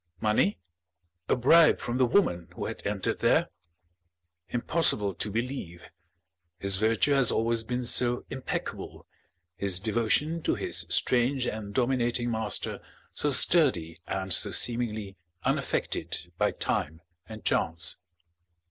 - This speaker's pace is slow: Yes, slow, 120 wpm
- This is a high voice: No, low, 115 Hz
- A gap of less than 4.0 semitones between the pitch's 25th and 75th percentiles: No, average, 4.4 semitones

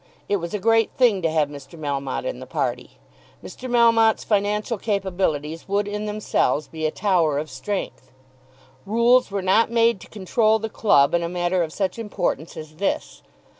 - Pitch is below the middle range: No, high, 195 Hz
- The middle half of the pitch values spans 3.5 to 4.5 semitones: No, wide, 5.5 semitones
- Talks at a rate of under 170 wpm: No, average, 175 wpm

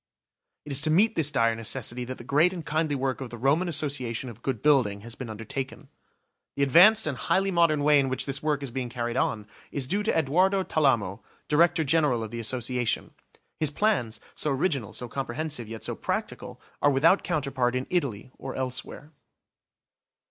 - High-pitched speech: No, low, 135 Hz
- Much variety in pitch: No, average, 4.3 semitones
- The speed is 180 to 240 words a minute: Yes, average, 185 wpm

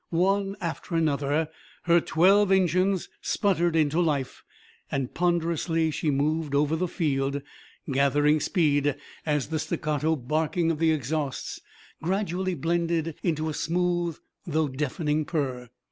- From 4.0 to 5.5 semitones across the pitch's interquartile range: No, average, 2.8 semitones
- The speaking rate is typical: No, slow, 125 wpm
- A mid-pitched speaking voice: Yes, medium, 160 Hz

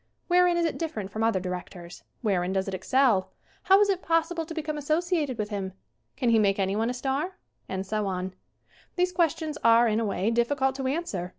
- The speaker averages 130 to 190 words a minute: No, average, 200 wpm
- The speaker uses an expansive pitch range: Yes, wide, 8.6 semitones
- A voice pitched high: Yes, high, 235 Hz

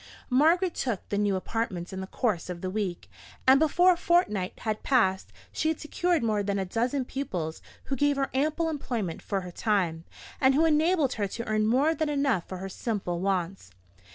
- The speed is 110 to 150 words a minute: No, average, 195 wpm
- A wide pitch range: Yes, wide, 7.2 semitones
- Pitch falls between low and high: No, high, 225 Hz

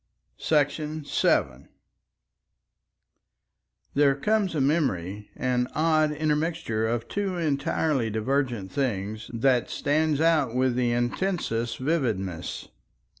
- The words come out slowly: Yes, slow, 95 wpm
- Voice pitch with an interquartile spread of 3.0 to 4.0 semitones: No, average, 5.2 semitones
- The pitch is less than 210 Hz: Yes, low, 135 Hz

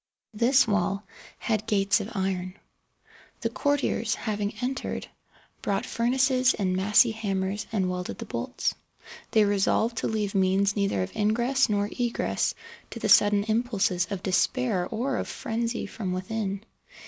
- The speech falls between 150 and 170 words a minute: No, average, 140 wpm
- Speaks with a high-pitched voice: Yes, high, 210 Hz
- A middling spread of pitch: Yes, average, 3.2 semitones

